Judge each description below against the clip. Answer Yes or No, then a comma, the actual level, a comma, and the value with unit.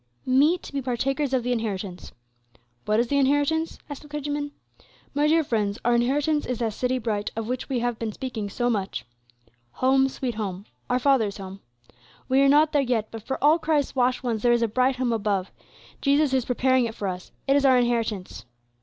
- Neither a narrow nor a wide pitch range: Yes, average, 3.8 semitones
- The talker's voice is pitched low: No, very high, 250 Hz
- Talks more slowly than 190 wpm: No, fast, 205 wpm